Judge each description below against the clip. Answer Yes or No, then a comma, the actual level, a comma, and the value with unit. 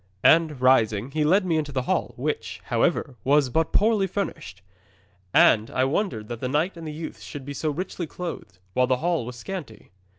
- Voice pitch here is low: No, medium, 145 Hz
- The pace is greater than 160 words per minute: Yes, average, 195 wpm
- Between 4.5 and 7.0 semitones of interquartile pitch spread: Yes, average, 4.8 semitones